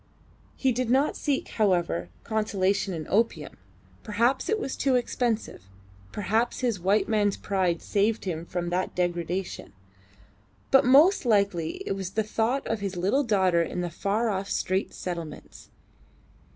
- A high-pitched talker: Yes, high, 200 Hz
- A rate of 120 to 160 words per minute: Yes, average, 145 wpm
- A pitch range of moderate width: Yes, average, 4.3 semitones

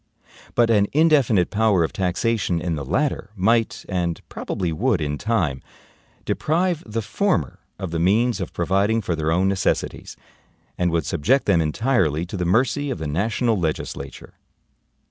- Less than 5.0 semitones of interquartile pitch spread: No, wide, 5.5 semitones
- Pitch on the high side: No, very low, 95 Hz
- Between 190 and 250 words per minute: No, average, 155 wpm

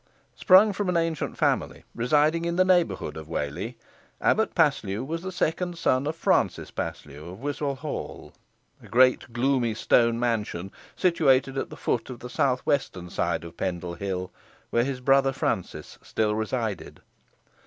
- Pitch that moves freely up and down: Yes, wide, 6.7 semitones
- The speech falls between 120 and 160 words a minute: Yes, average, 155 wpm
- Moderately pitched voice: No, low, 130 Hz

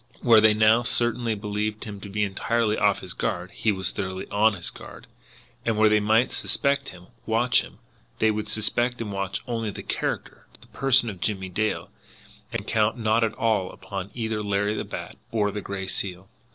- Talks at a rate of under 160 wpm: No, average, 190 wpm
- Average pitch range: No, narrow, 2.3 semitones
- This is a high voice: No, low, 105 Hz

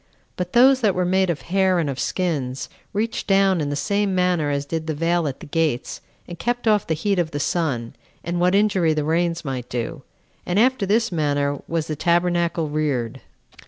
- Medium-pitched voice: Yes, medium, 170 Hz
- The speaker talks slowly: No, average, 200 wpm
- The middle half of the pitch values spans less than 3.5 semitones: No, average, 4.4 semitones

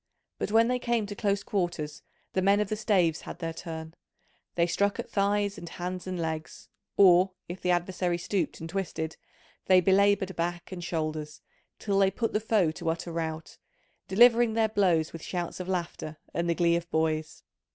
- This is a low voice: No, medium, 180 Hz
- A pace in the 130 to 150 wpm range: No, average, 185 wpm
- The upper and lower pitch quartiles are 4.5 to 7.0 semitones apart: No, average, 3.3 semitones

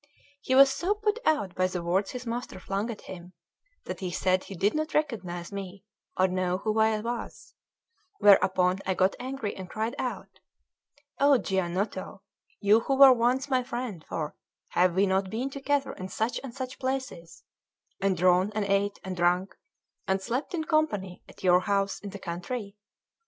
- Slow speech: No, average, 175 wpm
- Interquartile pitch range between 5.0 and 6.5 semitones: Yes, wide, 5.4 semitones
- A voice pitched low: No, high, 200 Hz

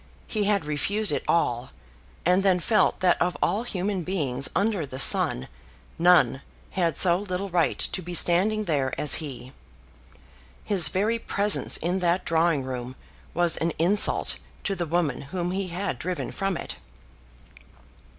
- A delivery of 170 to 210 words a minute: No, average, 150 wpm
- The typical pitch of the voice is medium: Yes, medium, 175 Hz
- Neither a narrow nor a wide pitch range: Yes, average, 4.2 semitones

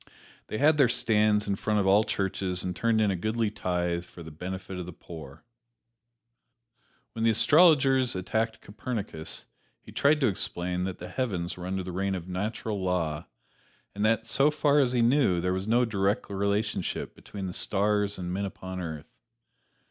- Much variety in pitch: No, average, 3.7 semitones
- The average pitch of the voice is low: Yes, low, 100 Hz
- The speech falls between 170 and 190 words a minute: Yes, average, 180 wpm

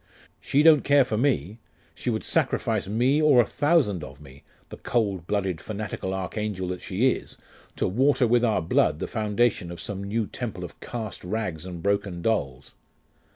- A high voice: No, low, 105 Hz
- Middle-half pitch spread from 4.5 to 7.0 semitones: Yes, average, 5.0 semitones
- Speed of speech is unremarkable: Yes, average, 175 wpm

